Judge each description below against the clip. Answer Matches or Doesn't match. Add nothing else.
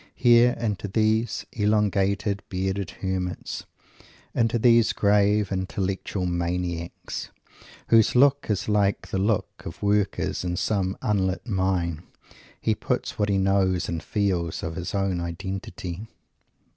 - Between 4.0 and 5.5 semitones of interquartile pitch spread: Doesn't match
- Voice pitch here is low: Matches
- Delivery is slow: Matches